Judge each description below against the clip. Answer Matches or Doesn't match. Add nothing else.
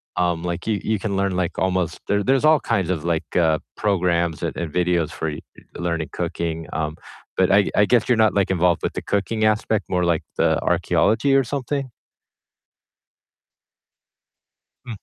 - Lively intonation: Doesn't match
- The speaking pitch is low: Matches